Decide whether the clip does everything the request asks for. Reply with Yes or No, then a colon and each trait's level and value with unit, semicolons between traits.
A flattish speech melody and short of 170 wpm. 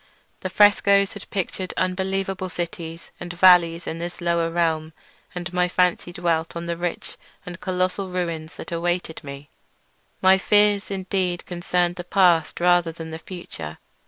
Yes: narrow, 1.8 semitones; average, 155 wpm